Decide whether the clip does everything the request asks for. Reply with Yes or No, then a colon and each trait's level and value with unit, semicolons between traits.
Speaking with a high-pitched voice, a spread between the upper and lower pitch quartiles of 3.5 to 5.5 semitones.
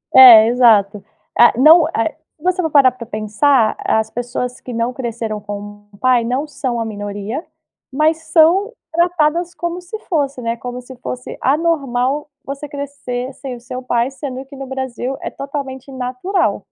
Yes: very high, 255 Hz; average, 3.8 semitones